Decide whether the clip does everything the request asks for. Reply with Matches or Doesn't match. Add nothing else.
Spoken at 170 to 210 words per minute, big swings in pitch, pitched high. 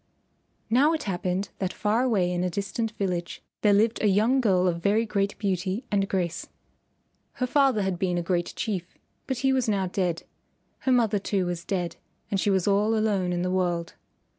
Doesn't match